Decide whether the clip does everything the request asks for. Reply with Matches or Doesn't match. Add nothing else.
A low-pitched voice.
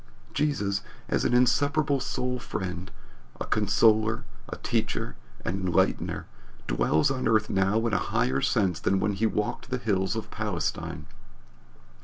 Matches